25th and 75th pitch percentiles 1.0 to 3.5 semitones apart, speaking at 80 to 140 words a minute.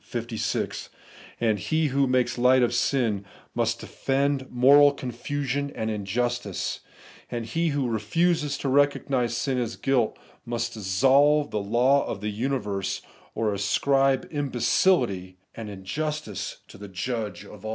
No: average, 4.4 semitones; slow, 135 wpm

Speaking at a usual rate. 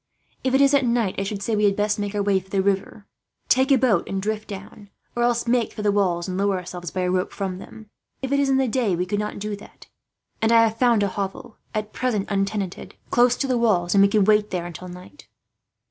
No: fast, 250 wpm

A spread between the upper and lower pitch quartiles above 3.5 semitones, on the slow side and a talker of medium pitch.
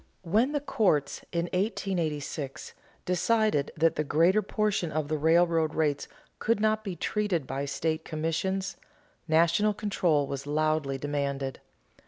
Yes: average, 4.8 semitones; slow, 130 wpm; medium, 165 Hz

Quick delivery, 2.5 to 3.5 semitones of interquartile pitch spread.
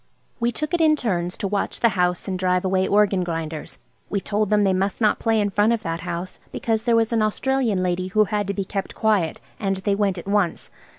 Yes: fast, 235 wpm; average, 2.9 semitones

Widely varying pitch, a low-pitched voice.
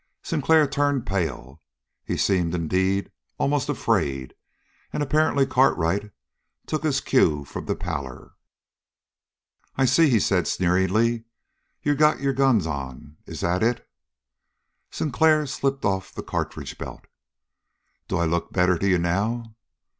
Yes: wide, 8.0 semitones; low, 100 Hz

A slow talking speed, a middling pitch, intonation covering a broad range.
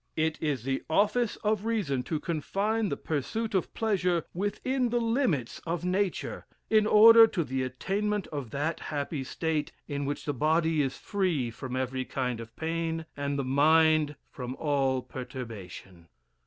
No: average, 155 wpm; medium, 160 Hz; wide, 7.0 semitones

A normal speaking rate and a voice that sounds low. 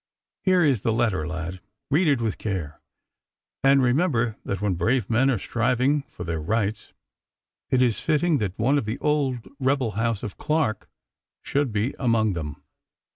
Yes: average, 165 wpm; low, 115 Hz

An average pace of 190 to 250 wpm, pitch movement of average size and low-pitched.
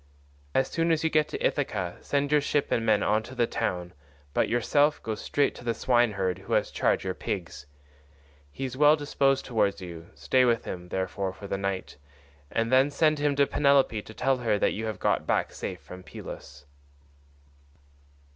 No: average, 195 wpm; wide, 6.5 semitones; low, 115 Hz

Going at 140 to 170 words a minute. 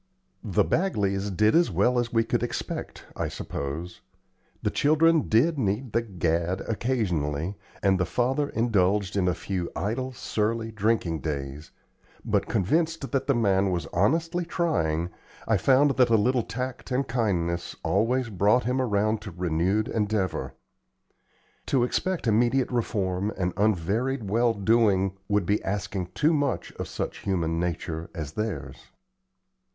Yes: average, 145 wpm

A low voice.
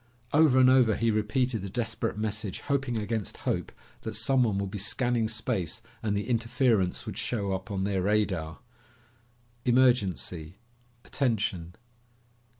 Yes: low, 110 Hz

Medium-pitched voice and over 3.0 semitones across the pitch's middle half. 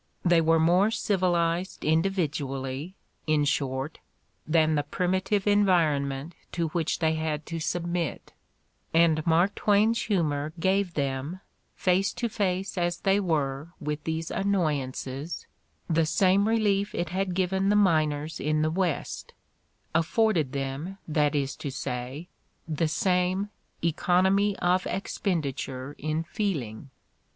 Yes: medium, 165 Hz; average, 3.9 semitones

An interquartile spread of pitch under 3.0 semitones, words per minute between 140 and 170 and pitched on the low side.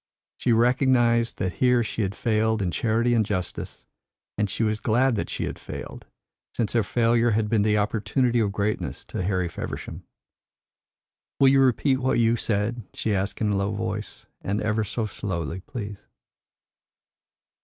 Yes: narrow, 2.5 semitones; average, 165 wpm; low, 110 Hz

